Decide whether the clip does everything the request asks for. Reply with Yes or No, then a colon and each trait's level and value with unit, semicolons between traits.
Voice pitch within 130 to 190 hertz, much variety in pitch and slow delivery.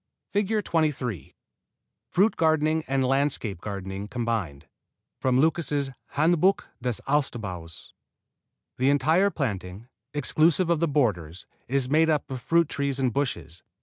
Yes: low, 135 Hz; wide, 6.1 semitones; slow, 125 wpm